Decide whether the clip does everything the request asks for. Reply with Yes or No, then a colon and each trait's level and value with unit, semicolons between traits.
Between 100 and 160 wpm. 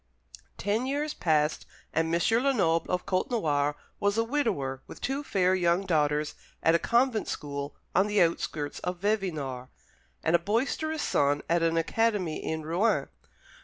Yes: average, 150 wpm